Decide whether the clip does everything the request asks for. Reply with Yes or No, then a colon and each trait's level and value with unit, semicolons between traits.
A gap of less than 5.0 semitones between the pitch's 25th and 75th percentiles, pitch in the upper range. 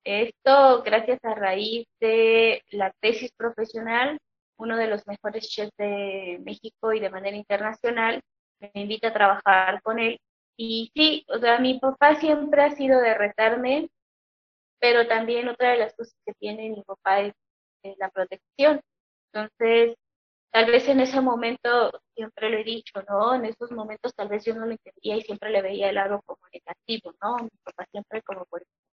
Yes: average, 2.9 semitones; high, 225 Hz